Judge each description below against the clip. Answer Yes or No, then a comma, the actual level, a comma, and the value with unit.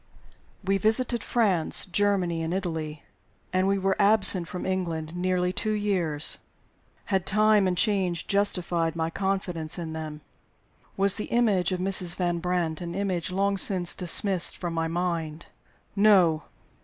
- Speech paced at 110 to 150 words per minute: Yes, average, 145 wpm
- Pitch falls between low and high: Yes, medium, 180 Hz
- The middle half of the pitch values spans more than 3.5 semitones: No, average, 2.9 semitones